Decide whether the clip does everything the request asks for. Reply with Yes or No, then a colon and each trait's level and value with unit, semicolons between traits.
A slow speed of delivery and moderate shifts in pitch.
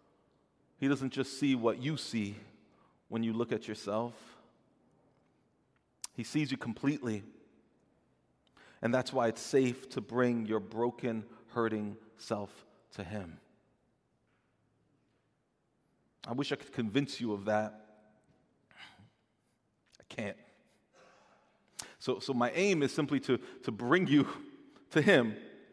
Yes: slow, 120 wpm; average, 4.1 semitones